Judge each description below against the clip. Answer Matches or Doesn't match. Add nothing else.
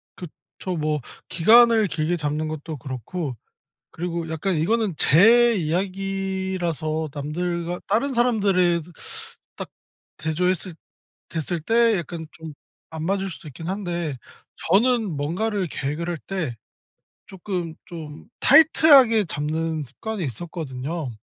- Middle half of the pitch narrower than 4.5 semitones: Matches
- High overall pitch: Doesn't match